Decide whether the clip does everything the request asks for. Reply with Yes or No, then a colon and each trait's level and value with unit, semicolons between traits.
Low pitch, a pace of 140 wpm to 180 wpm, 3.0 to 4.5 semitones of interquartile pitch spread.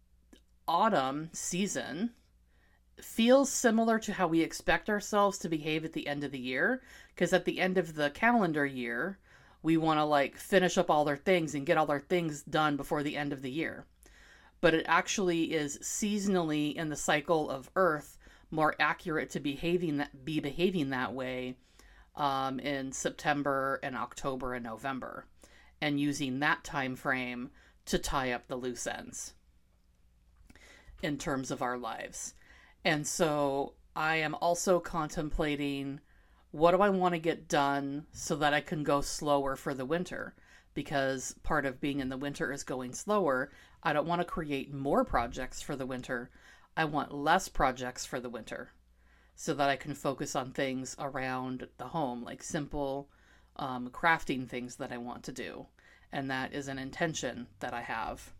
No: medium, 145 Hz; average, 170 wpm; average, 4.1 semitones